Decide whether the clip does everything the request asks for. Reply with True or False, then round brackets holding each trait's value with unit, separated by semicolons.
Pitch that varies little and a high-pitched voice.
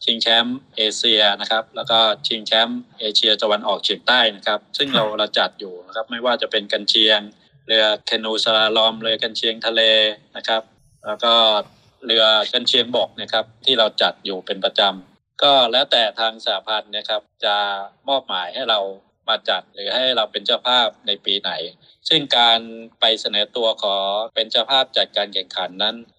False (1.3 semitones; 110 Hz)